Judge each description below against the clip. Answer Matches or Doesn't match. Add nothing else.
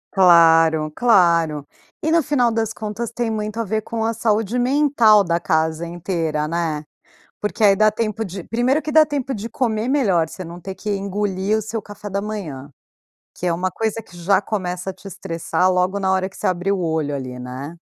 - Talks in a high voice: Matches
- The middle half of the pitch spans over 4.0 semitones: Matches